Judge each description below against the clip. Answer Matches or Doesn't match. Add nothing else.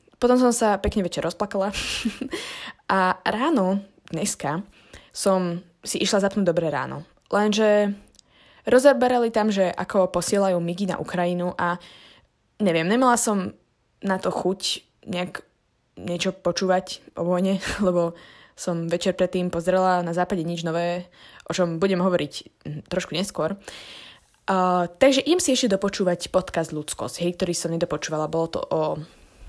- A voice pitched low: Doesn't match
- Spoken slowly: Doesn't match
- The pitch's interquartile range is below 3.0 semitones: Matches